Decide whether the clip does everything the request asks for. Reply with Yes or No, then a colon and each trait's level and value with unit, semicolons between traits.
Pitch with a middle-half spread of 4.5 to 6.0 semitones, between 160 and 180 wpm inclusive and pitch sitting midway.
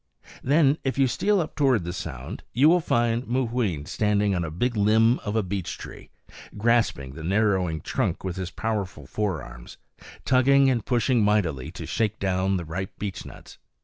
No: average, 5.1 semitones; average, 170 wpm; low, 105 Hz